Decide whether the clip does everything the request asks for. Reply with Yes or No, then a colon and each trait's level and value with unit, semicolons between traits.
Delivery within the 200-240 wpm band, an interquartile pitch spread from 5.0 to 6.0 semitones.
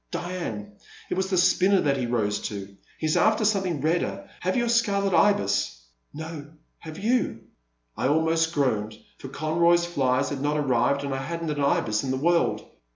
Yes: fast, 205 wpm; wide, 5.6 semitones